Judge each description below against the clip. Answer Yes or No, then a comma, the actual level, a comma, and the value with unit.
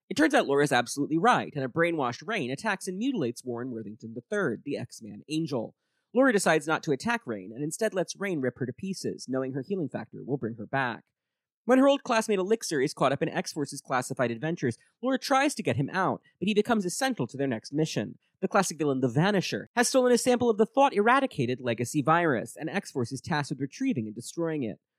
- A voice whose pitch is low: No, medium, 155 Hz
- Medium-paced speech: No, fast, 220 wpm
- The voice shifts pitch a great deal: Yes, wide, 8.8 semitones